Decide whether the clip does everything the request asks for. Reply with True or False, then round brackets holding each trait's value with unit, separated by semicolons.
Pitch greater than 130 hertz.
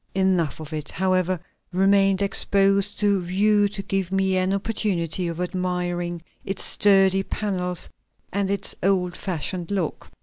True (190 Hz)